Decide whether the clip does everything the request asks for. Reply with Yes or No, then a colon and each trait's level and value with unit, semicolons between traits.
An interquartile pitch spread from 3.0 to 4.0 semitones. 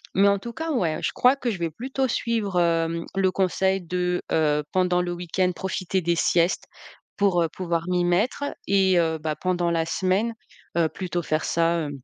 No: narrow, 2.5 semitones